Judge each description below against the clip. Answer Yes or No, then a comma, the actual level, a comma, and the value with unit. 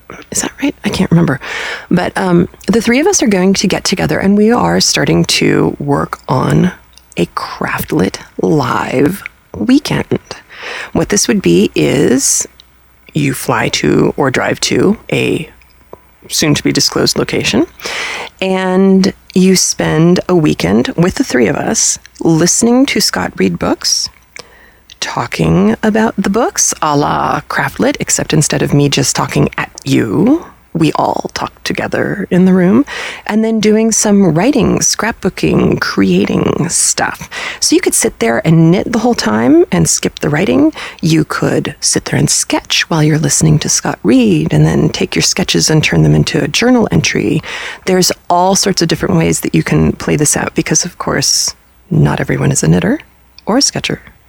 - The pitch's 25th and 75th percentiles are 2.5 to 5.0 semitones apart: No, wide, 5.5 semitones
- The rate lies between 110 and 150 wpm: No, average, 165 wpm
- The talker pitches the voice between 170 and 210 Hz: Yes, high, 190 Hz